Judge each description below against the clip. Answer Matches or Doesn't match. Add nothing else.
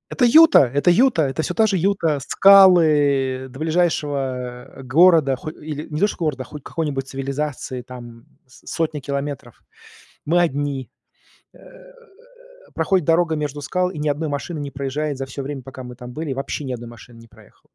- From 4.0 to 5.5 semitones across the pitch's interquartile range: Doesn't match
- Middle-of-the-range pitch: Matches